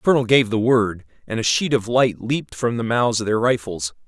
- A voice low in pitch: Yes, low, 115 Hz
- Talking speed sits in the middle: No, fast, 250 wpm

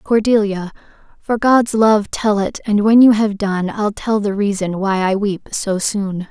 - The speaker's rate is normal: Yes, average, 190 wpm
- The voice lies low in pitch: No, high, 205 Hz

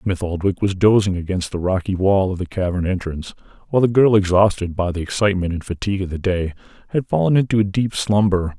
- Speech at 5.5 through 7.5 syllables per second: Yes, 6.0 syllables/s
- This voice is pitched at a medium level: No, very low, 95 Hz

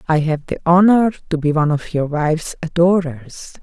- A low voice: No, medium, 165 Hz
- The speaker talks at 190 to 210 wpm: No, average, 180 wpm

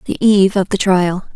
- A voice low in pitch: No, high, 195 Hz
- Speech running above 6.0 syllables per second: No, 5.4 syllables/s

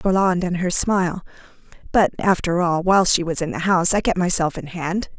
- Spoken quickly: Yes, fast, 210 wpm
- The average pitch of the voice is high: No, medium, 180 Hz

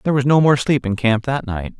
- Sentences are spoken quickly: Yes, fast, 300 wpm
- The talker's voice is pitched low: Yes, low, 125 Hz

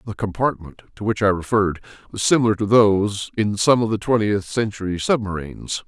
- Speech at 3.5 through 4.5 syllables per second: No, 5.7 syllables/s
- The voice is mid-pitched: No, low, 105 Hz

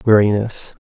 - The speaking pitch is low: Yes, low, 105 Hz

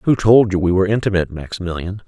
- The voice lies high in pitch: No, very low, 95 Hz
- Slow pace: No, average, 200 wpm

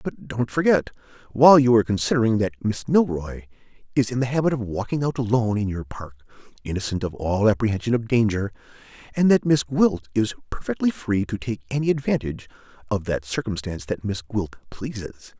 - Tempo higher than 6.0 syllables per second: No, 5.8 syllables/s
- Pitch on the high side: No, low, 115 Hz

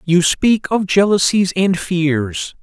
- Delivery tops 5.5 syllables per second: No, 3.2 syllables/s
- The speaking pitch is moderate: Yes, medium, 180 Hz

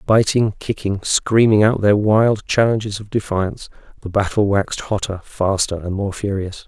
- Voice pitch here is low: Yes, low, 100 Hz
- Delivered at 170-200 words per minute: No, average, 155 wpm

